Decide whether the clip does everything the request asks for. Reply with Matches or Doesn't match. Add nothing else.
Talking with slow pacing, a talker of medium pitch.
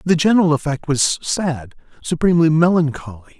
Matches